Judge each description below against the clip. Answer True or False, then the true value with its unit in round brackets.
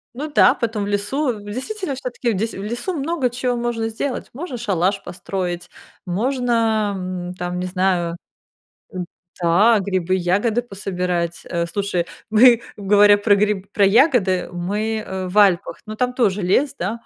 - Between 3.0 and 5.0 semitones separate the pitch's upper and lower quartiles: True (4.4 semitones)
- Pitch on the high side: True (205 Hz)